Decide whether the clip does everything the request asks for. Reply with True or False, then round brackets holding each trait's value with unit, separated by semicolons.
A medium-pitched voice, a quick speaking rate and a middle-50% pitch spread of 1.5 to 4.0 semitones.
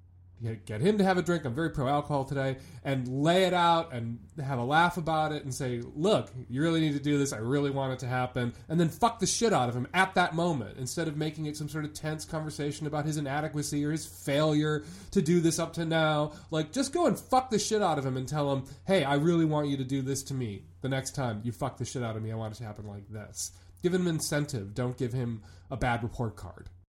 False (145 Hz; 260 wpm; 4.5 semitones)